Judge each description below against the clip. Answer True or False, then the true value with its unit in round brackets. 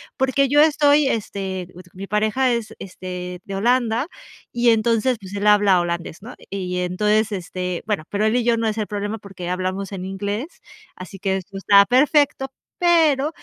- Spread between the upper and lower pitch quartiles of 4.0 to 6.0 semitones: True (4.4 semitones)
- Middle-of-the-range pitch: False (210 Hz)